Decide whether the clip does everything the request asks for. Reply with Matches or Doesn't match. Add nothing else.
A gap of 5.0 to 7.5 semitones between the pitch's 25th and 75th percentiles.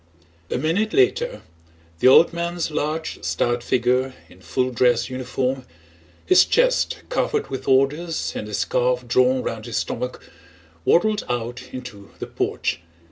Matches